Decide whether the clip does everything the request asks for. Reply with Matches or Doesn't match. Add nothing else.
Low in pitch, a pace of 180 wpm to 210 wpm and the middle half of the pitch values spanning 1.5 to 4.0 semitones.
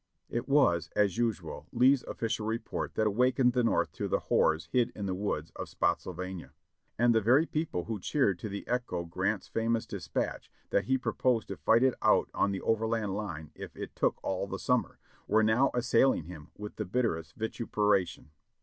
Doesn't match